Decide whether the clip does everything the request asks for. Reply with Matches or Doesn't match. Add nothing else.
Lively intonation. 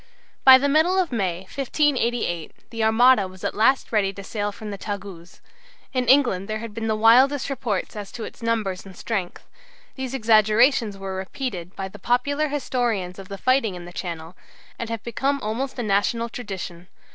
Doesn't match